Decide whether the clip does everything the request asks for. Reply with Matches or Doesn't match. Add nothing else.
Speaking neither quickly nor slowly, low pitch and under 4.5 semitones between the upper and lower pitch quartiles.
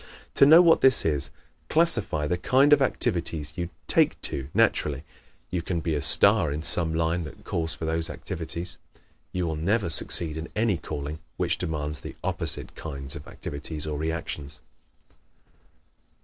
Matches